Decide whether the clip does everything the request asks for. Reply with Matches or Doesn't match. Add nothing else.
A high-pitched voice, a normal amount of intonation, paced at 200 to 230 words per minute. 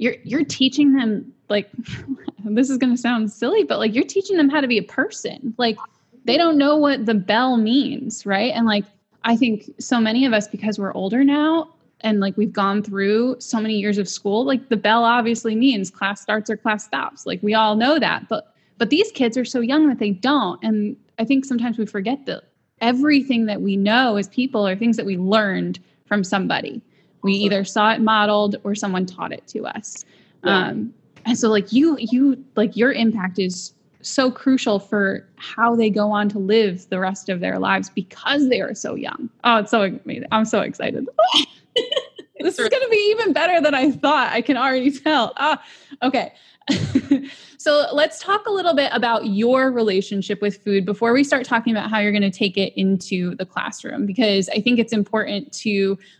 Matches